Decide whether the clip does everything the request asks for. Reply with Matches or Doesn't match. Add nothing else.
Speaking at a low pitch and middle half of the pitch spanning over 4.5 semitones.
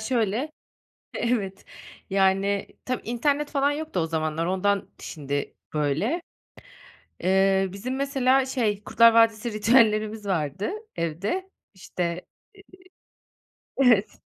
Doesn't match